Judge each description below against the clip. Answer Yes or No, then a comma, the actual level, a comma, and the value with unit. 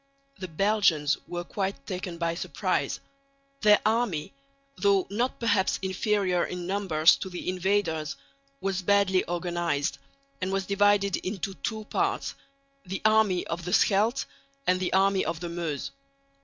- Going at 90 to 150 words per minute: Yes, average, 140 wpm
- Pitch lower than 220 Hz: Yes, high, 190 Hz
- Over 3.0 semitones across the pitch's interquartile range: No, narrow, 2.6 semitones